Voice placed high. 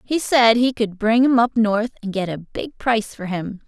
Yes: high, 225 Hz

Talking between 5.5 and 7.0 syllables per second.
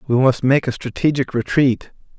No: 5.0 syllables/s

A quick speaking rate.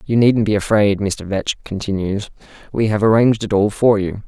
No: average, 195 wpm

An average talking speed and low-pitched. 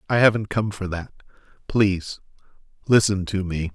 Yes: average, 145 wpm; very low, 95 Hz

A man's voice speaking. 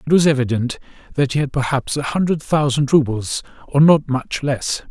Yes: male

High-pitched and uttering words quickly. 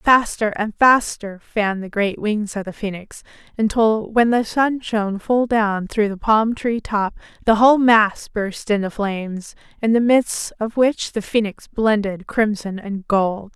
No: high, 215 Hz; average, 175 wpm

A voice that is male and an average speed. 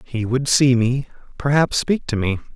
Yes: male; average, 190 wpm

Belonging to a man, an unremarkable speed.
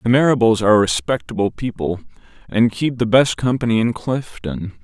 Yes: male; average, 150 wpm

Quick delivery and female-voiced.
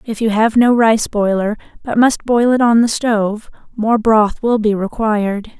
No: average, 195 wpm; female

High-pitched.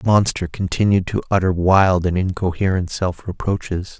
No: very low, 90 Hz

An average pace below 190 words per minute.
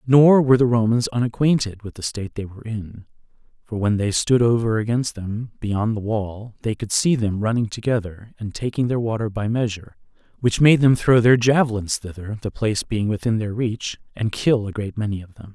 No: fast, 205 wpm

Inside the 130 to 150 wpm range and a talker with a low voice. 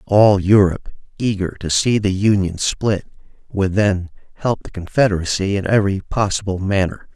Yes: average, 145 wpm; low, 100 Hz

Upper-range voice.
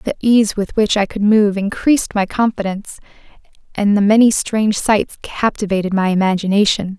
Yes: high, 205 Hz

